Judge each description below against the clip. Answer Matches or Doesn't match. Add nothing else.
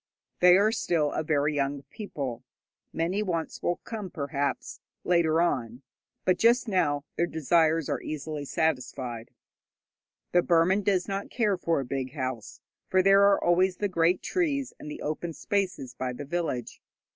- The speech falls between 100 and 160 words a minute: Matches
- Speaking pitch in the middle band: Matches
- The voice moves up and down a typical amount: Matches